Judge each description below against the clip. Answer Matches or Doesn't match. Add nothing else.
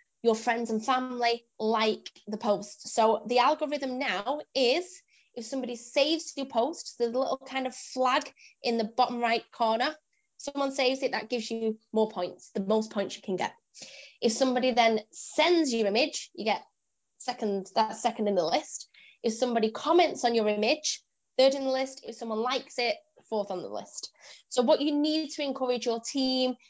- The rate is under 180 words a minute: Doesn't match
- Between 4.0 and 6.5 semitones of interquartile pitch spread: Doesn't match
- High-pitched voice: Matches